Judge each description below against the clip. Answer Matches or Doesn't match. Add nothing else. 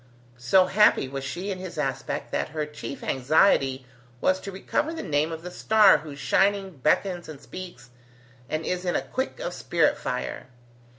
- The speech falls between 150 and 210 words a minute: Matches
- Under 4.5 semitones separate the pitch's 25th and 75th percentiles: Doesn't match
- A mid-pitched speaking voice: Matches